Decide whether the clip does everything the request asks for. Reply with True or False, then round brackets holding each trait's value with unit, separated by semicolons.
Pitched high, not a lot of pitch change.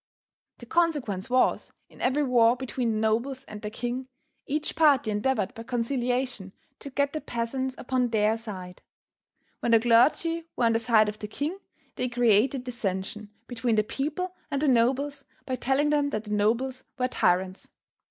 False (245 Hz; 3.6 semitones)